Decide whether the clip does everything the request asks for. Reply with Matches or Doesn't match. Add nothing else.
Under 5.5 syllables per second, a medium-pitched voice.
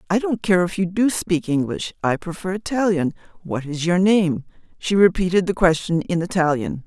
Matches